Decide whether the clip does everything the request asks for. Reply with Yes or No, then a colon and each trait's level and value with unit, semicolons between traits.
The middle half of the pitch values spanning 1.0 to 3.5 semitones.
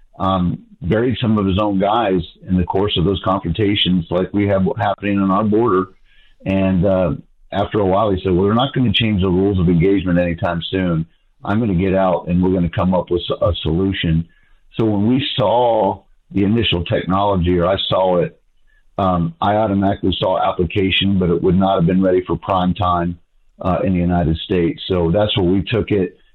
Yes: narrow, 2.5 semitones